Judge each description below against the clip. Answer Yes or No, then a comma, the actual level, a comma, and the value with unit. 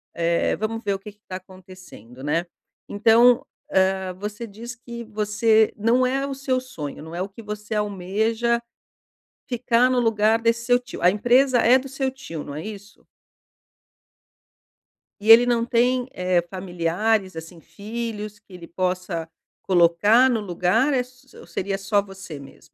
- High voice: Yes, high, 210 Hz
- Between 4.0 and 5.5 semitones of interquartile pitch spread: Yes, average, 4.3 semitones